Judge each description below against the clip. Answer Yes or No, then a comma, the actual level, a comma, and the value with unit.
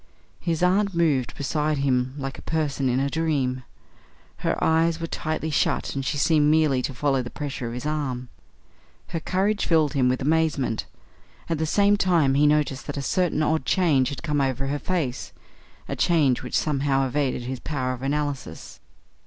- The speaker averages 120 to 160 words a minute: No, average, 180 wpm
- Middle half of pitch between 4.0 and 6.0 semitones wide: No, average, 3.2 semitones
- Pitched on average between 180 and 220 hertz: No, medium, 145 Hz